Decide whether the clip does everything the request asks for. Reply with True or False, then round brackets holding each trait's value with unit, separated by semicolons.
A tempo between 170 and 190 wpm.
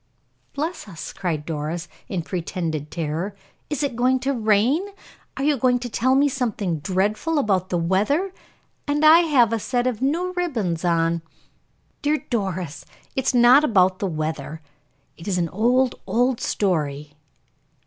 False (155 wpm)